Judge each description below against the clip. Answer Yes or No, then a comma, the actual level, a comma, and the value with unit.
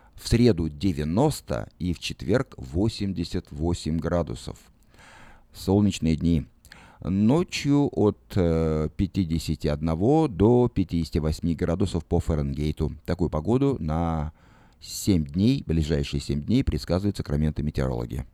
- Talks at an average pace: No, slow, 95 wpm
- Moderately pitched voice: No, very low, 85 Hz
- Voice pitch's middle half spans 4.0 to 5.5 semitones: Yes, average, 4.5 semitones